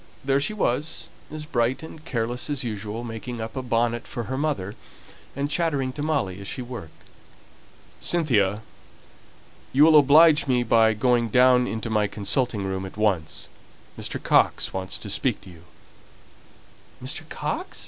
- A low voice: Yes, low, 120 Hz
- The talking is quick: No, average, 155 wpm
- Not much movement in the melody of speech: No, average, 4.8 semitones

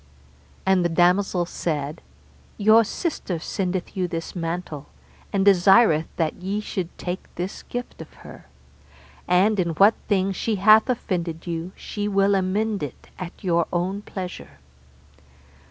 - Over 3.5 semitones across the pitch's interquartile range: No, average, 2.8 semitones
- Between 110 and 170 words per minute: Yes, average, 140 wpm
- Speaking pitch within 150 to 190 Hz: Yes, medium, 185 Hz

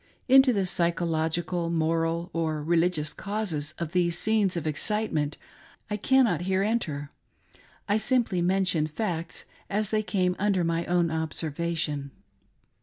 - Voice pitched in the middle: Yes, medium, 170 Hz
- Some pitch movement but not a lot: Yes, average, 3.9 semitones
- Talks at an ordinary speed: No, slow, 130 wpm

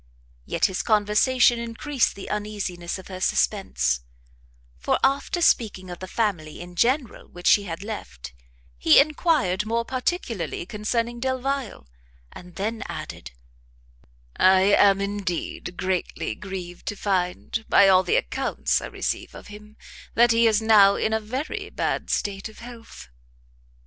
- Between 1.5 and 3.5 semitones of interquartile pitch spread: No, average, 3.9 semitones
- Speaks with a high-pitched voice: Yes, high, 210 Hz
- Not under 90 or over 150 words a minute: Yes, average, 140 wpm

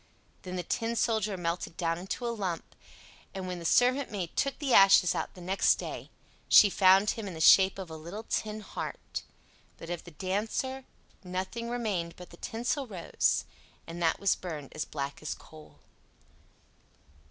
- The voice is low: No, high, 190 Hz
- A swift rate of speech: No, average, 170 wpm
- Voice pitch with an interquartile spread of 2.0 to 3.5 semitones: No, average, 4.4 semitones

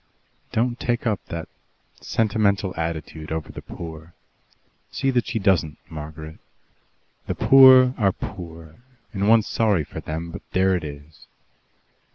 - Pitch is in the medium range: No, very low, 90 Hz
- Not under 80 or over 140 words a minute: Yes, slow, 135 wpm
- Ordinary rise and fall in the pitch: No, wide, 5.8 semitones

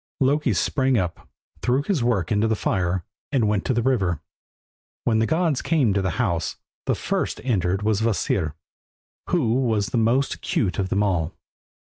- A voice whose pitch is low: Yes, low, 110 Hz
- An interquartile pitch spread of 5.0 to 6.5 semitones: Yes, average, 5.3 semitones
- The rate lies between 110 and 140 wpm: No, average, 175 wpm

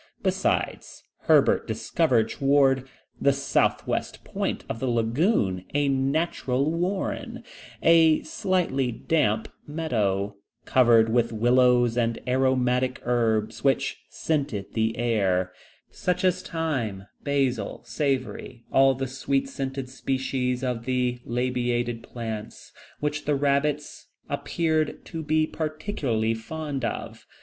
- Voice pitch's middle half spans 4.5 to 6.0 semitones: No, average, 4.1 semitones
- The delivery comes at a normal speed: No, slow, 110 wpm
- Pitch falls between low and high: No, low, 130 Hz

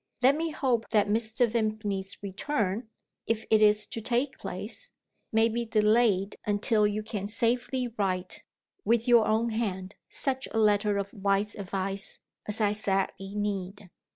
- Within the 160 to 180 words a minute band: No, average, 150 wpm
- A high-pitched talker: Yes, high, 215 Hz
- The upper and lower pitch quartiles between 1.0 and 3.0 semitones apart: Yes, narrow, 2.5 semitones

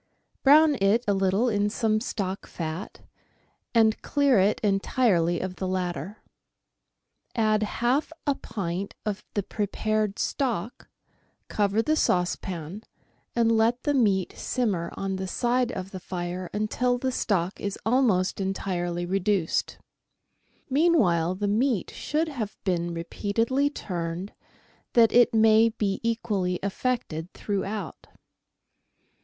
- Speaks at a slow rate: Yes, slow, 125 wpm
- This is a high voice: Yes, high, 205 Hz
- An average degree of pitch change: Yes, average, 4.1 semitones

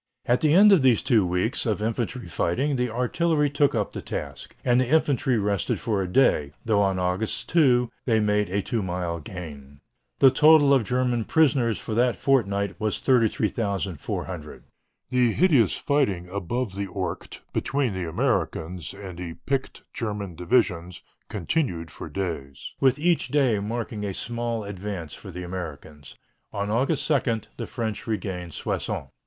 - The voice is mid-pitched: No, low, 110 Hz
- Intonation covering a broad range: Yes, wide, 5.8 semitones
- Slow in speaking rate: No, average, 160 wpm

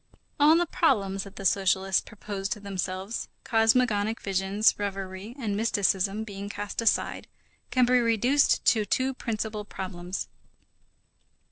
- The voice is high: Yes, high, 205 Hz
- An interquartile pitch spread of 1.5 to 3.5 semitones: Yes, average, 2.9 semitones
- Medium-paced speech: No, slow, 125 wpm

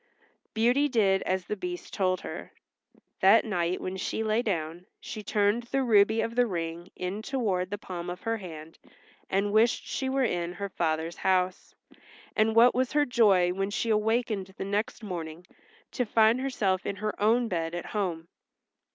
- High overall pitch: Yes, high, 200 Hz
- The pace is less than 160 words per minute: No, average, 175 wpm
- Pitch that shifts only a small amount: No, average, 4.0 semitones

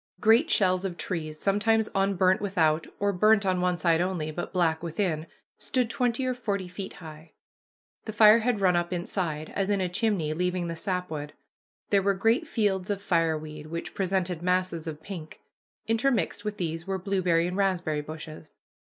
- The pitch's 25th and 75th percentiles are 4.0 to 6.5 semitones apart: No, average, 3.5 semitones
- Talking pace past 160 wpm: Yes, average, 170 wpm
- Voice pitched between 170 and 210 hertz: Yes, medium, 185 Hz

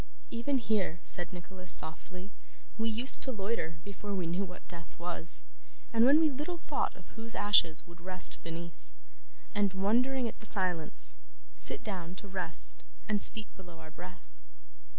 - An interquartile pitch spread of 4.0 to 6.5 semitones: Yes, average, 4.5 semitones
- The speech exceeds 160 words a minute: No, average, 155 wpm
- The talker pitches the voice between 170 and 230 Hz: Yes, high, 190 Hz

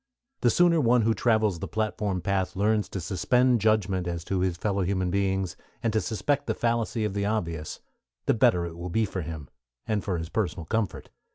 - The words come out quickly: No, average, 195 wpm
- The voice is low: Yes, low, 100 Hz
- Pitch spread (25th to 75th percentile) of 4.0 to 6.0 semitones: No, average, 3.6 semitones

